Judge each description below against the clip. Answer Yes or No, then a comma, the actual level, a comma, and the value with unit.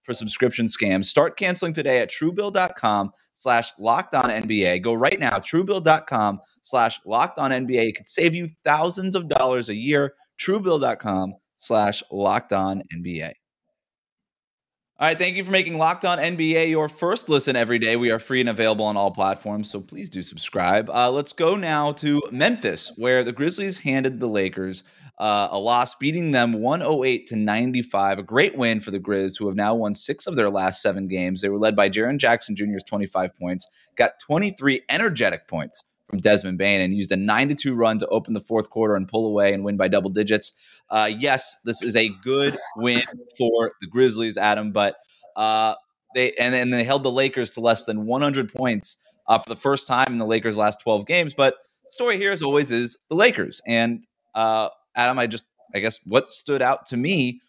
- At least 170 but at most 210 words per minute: Yes, average, 200 wpm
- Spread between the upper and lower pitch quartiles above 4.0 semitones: Yes, average, 5.3 semitones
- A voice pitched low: Yes, low, 115 Hz